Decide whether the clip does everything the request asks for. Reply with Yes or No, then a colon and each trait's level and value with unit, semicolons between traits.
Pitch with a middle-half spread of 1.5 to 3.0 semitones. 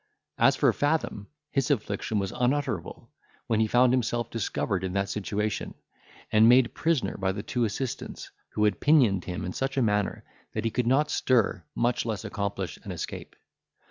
No: average, 3.9 semitones